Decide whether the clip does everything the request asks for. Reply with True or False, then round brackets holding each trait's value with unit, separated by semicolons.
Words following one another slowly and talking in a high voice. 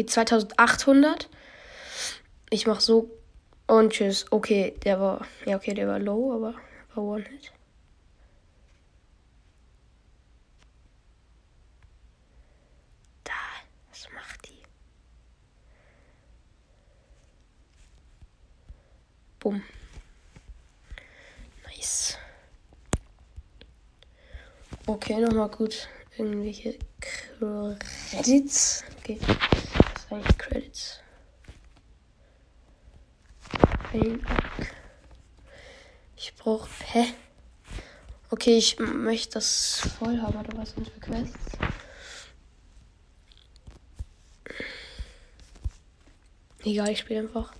True (65 wpm; 210 Hz)